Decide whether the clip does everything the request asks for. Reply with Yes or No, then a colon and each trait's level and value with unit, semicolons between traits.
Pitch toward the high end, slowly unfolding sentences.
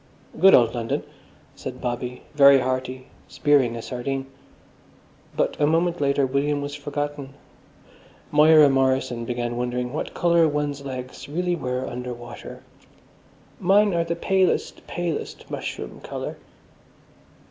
No: medium, 140 Hz; slow, 125 wpm